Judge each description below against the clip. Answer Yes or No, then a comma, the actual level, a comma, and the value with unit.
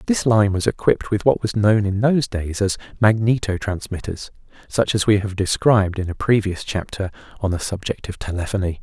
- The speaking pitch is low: Yes, low, 100 Hz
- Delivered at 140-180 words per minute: No, average, 190 wpm